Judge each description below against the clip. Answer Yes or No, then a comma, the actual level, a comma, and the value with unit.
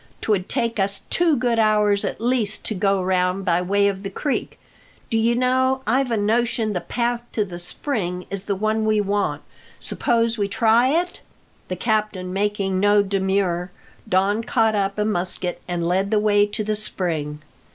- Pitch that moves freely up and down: No, average, 3.1 semitones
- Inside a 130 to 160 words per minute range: No, average, 180 wpm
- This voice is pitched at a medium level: No, high, 205 Hz